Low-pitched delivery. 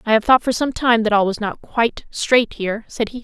No: high, 225 Hz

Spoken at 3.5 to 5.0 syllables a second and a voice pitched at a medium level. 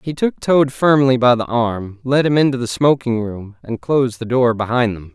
No: 4.8 syllables/s; low, 125 Hz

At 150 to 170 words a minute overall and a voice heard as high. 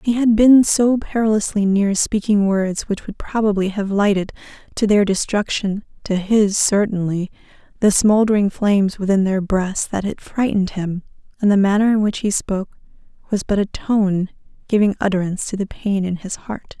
Yes: average, 165 wpm; high, 205 Hz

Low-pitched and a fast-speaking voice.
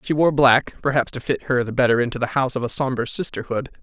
Yes: low, 130 Hz; fast, 235 wpm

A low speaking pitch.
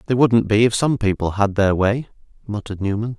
Yes: low, 110 Hz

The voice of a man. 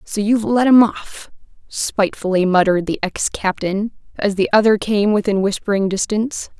No: female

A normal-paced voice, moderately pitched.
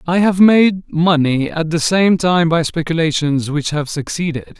Yes: average, 170 wpm; medium, 165 Hz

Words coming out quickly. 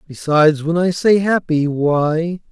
No: average, 145 wpm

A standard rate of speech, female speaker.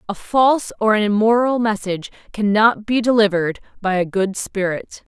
Yes: average, 150 wpm; female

